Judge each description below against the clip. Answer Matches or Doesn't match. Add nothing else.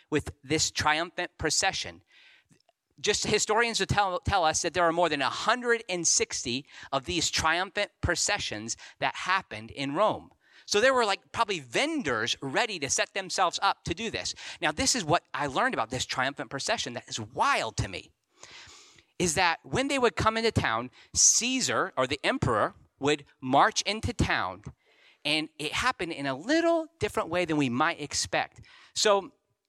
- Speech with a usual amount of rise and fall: Doesn't match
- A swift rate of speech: Doesn't match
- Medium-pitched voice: Matches